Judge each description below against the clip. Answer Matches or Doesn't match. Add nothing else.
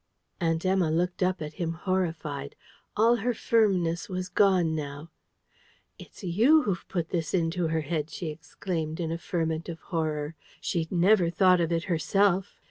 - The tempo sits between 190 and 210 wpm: Doesn't match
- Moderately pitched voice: Matches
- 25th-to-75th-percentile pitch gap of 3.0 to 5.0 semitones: Doesn't match